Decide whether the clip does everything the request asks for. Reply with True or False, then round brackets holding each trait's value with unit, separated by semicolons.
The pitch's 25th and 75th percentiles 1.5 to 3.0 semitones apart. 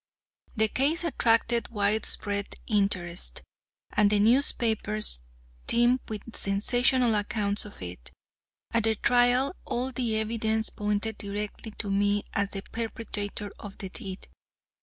True (2.4 semitones)